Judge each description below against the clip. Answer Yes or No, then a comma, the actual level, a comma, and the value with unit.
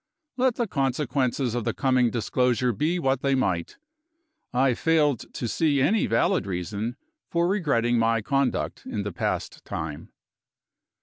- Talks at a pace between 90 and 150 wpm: Yes, average, 140 wpm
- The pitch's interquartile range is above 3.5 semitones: Yes, average, 4.4 semitones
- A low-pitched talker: Yes, low, 130 Hz